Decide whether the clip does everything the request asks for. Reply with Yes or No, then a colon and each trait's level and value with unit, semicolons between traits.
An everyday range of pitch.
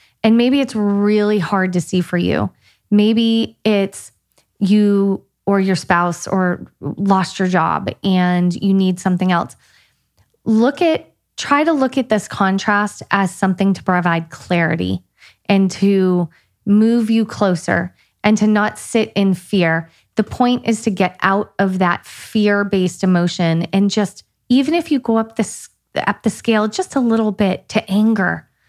Yes: average, 3.1 semitones